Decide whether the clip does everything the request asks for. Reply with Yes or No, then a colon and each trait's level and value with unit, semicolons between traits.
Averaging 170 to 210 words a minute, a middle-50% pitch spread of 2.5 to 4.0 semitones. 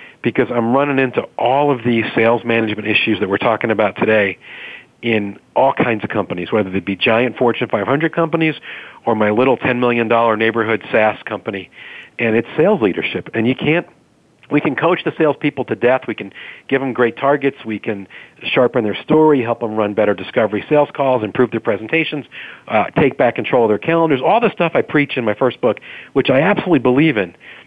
No: average, 195 wpm; average, 4.5 semitones